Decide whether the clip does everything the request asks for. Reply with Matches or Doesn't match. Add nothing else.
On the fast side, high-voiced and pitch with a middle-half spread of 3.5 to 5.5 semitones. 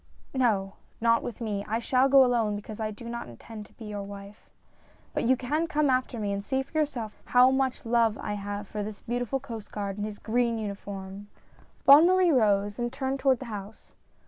Matches